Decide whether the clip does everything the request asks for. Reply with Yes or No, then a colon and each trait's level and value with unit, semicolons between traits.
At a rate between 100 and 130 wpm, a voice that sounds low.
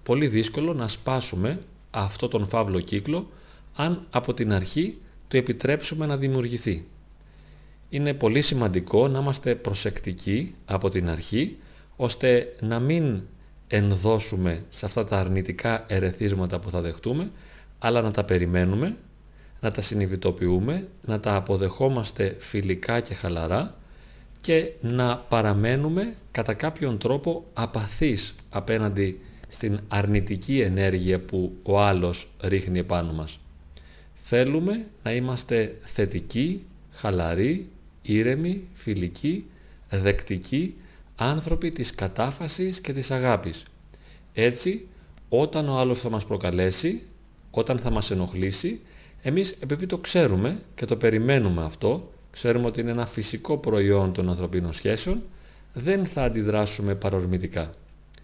Yes: slow, 115 wpm; low, 110 Hz